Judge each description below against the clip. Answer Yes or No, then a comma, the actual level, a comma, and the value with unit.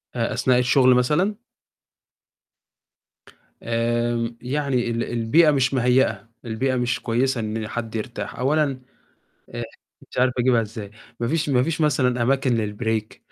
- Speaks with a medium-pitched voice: No, low, 125 Hz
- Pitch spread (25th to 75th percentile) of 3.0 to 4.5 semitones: No, narrow, 2.5 semitones